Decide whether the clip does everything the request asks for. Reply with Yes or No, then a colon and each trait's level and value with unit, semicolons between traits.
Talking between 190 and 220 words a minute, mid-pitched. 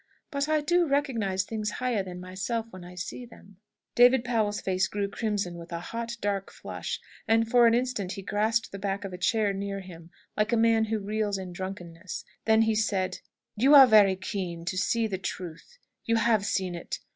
No: average, 200 wpm; high, 205 Hz